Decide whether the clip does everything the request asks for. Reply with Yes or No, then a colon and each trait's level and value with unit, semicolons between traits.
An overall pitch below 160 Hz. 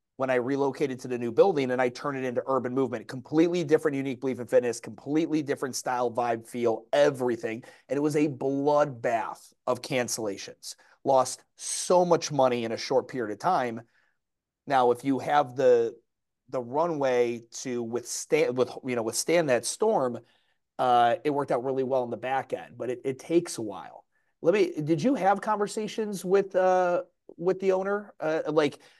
Yes: medium, 140 Hz